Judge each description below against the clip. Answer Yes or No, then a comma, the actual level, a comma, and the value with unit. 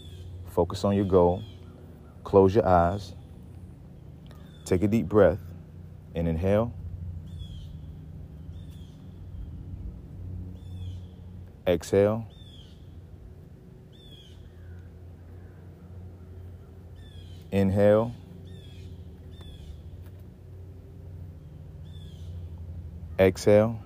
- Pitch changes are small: Yes, narrow, 1.3 semitones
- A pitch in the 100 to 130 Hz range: No, very low, 90 Hz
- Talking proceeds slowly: Yes, slow, 40 wpm